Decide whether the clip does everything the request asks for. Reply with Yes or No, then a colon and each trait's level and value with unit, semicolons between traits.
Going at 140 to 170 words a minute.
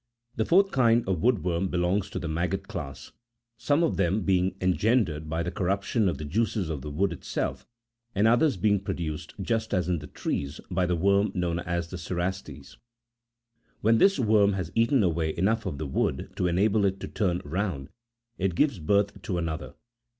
No: average, 185 wpm